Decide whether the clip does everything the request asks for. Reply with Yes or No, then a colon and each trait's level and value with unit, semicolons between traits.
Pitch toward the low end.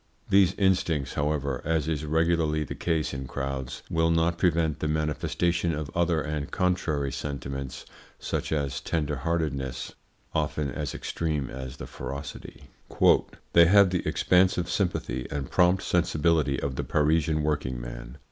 Yes: very low, 75 Hz